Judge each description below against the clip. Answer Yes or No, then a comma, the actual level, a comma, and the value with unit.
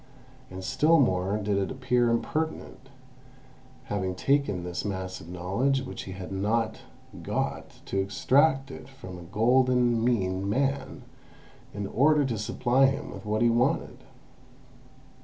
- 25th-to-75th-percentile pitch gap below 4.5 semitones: No, wide, 5.6 semitones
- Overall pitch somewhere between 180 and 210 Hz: No, low, 115 Hz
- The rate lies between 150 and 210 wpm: No, average, 140 wpm